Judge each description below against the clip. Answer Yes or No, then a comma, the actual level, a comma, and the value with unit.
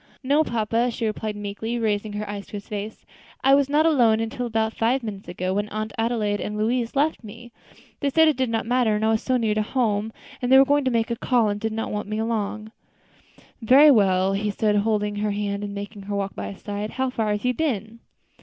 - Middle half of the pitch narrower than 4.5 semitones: Yes, average, 2.9 semitones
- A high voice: Yes, high, 220 Hz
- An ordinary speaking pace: No, fast, 240 wpm